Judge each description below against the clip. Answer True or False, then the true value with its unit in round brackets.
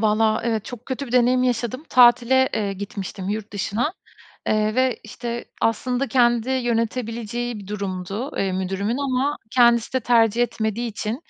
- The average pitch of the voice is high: True (235 Hz)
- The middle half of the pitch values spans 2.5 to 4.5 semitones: True (2.8 semitones)